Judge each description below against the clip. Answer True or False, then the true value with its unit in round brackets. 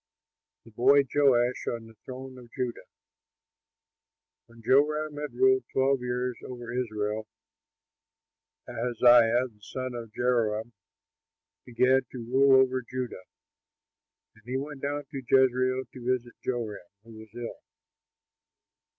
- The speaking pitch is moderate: False (125 Hz)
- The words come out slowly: True (120 wpm)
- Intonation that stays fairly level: True (2.1 semitones)